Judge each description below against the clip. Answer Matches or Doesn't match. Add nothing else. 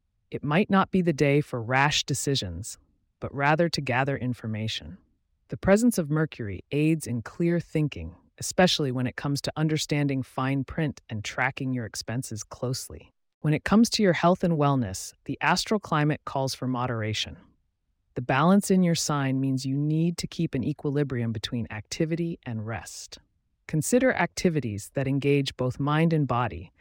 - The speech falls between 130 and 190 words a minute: Matches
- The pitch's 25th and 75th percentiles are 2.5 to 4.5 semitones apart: Doesn't match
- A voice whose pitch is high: Doesn't match